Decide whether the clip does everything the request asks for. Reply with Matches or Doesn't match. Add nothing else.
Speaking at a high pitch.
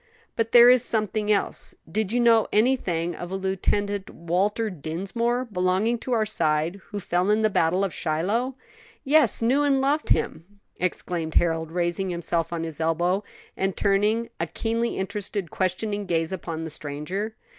Matches